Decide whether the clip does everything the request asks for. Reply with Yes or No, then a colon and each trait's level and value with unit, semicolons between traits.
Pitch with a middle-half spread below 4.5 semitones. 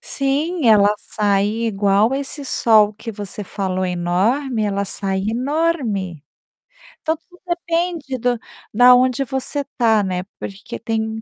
No: average, 5.3 semitones